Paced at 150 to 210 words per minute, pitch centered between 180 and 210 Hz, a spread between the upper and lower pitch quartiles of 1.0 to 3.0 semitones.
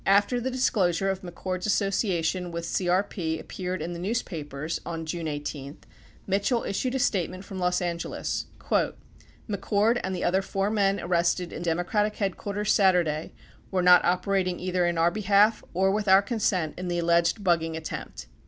Yes: average, 160 wpm; medium, 185 Hz; average, 2.7 semitones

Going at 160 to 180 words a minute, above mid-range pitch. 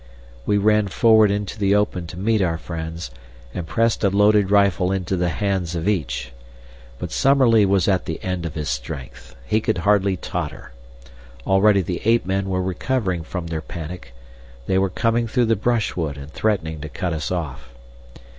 No: average, 175 wpm; very low, 95 Hz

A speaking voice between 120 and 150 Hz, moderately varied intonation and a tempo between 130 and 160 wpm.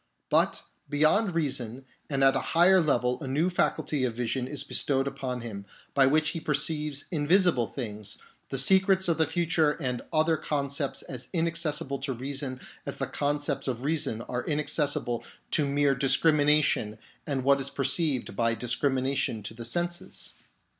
Yes: medium, 140 Hz; average, 3.5 semitones; average, 155 wpm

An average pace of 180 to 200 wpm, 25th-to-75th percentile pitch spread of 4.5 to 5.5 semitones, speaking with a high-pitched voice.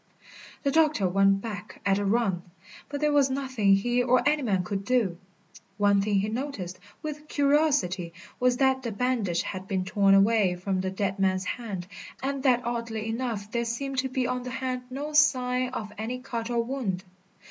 Yes: average, 185 wpm; average, 4.8 semitones; high, 235 Hz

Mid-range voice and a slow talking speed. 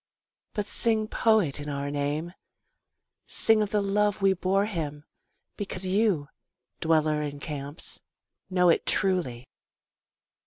Yes: medium, 180 Hz; slow, 120 wpm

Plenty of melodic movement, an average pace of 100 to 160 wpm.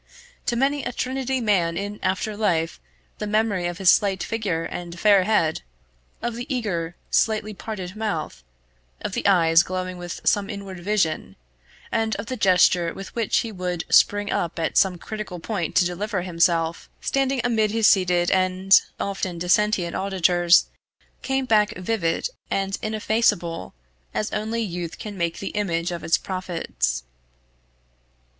No: average, 3.7 semitones; average, 150 wpm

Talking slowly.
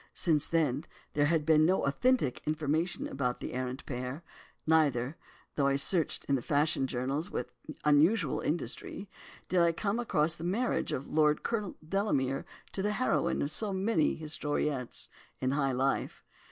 No: average, 145 wpm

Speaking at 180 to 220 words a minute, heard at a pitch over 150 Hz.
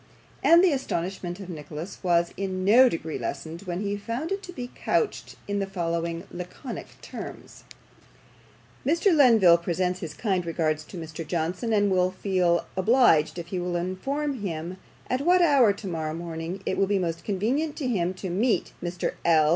No: average, 170 wpm; medium, 185 Hz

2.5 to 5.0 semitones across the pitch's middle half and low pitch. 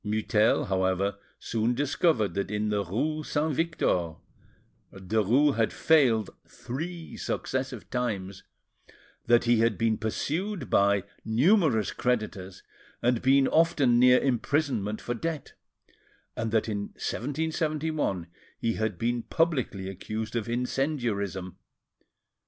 No: wide, 5.4 semitones; low, 115 Hz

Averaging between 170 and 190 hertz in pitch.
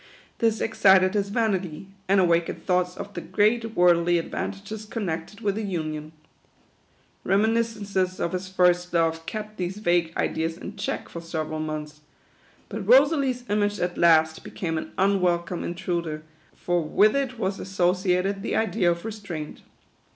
Yes: medium, 185 Hz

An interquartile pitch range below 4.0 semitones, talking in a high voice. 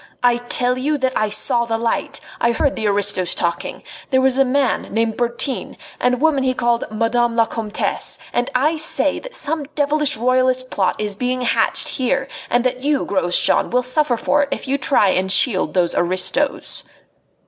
Yes: average, 3.2 semitones; very high, 250 Hz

